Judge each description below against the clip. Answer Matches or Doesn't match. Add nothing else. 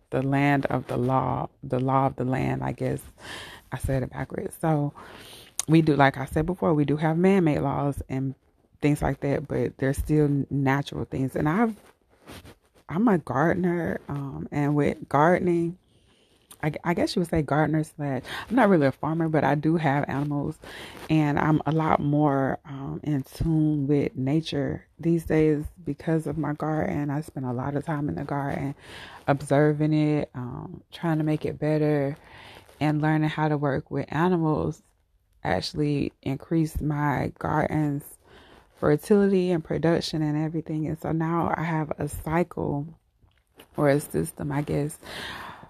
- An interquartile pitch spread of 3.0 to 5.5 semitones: Doesn't match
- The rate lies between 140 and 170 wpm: Matches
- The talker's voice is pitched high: Doesn't match